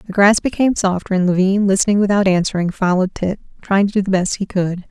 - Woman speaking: Yes, female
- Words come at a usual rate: No, fast, 220 wpm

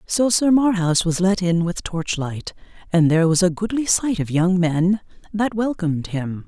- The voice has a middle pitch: Yes, medium, 180 Hz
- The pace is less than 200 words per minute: Yes, average, 185 wpm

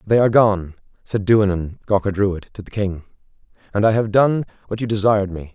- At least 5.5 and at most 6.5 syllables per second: Yes, 5.8 syllables/s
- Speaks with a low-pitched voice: Yes, low, 105 Hz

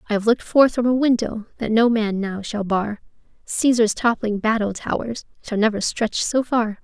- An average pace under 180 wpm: No, average, 195 wpm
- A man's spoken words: No, female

